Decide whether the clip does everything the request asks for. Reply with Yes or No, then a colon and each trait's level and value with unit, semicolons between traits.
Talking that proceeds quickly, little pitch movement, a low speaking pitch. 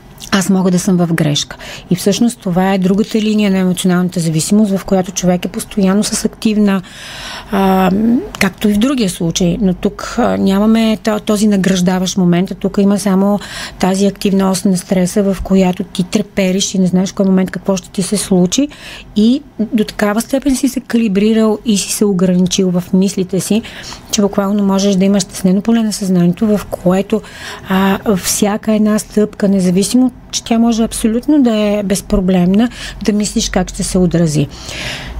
No: fast, 175 wpm; narrow, 2.2 semitones; high, 200 Hz